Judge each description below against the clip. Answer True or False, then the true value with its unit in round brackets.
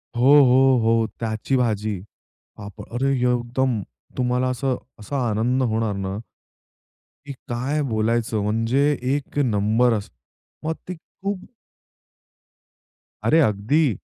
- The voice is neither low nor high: False (120 Hz)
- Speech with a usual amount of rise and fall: True (3.6 semitones)